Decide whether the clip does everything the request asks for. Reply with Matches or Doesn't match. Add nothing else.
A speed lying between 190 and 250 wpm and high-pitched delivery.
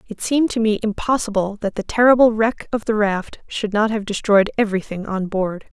Matches